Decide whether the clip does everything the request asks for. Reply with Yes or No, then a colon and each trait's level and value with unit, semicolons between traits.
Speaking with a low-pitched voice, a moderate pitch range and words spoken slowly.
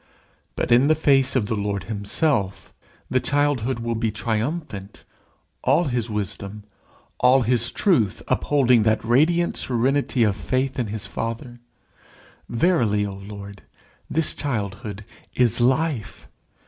Yes: low, 120 Hz; average, 4.4 semitones; slow, 125 wpm